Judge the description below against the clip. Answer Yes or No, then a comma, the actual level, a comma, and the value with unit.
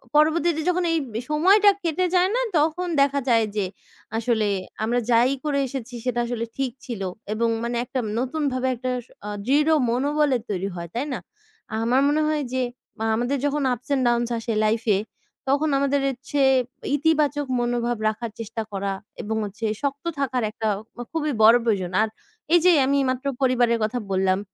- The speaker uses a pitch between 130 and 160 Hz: No, very high, 255 Hz